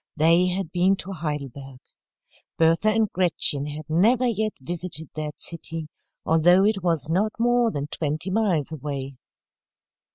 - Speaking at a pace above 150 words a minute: No, slow, 135 wpm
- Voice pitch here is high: No, medium, 165 Hz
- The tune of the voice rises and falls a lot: No, average, 4.5 semitones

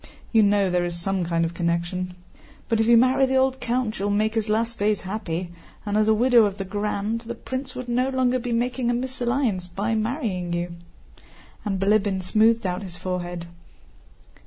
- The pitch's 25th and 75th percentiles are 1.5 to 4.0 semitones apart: No, average, 4.5 semitones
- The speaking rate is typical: Yes, average, 190 wpm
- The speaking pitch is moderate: No, high, 215 Hz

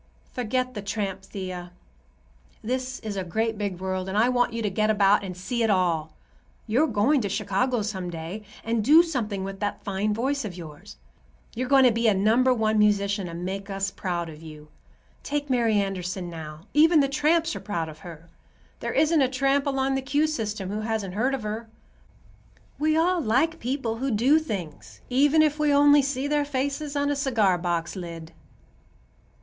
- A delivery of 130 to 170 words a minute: No, average, 190 wpm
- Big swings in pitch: Yes, wide, 6.1 semitones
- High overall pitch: Yes, high, 220 Hz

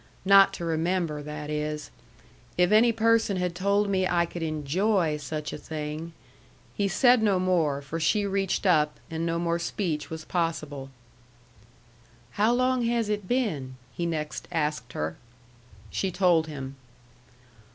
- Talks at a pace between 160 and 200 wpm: No, average, 150 wpm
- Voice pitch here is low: No, medium, 170 Hz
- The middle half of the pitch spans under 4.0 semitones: No, average, 4.6 semitones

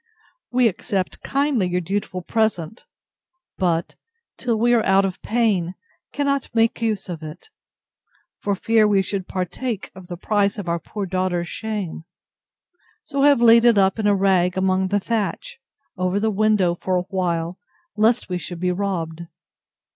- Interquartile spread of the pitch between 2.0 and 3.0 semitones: No, average, 3.5 semitones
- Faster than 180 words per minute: No, average, 160 wpm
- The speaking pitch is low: No, high, 195 Hz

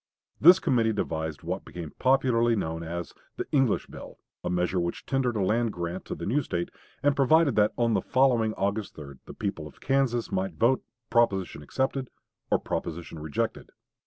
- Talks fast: No, average, 175 wpm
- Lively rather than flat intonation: Yes, wide, 6.8 semitones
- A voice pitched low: Yes, low, 110 Hz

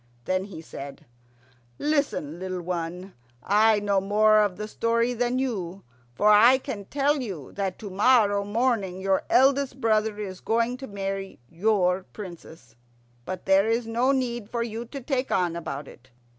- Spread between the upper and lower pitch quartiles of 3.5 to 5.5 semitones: Yes, average, 4.2 semitones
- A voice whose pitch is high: Yes, high, 210 Hz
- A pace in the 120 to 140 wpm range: No, average, 160 wpm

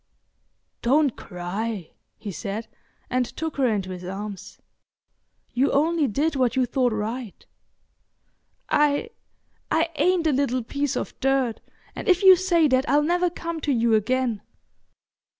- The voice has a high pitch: Yes, very high, 260 Hz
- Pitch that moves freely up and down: Yes, wide, 5.8 semitones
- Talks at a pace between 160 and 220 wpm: No, slow, 135 wpm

